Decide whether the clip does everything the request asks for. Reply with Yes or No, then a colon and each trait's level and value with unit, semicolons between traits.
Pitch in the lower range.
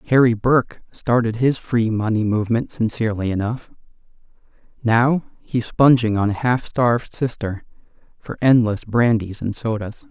Yes: low, 115 Hz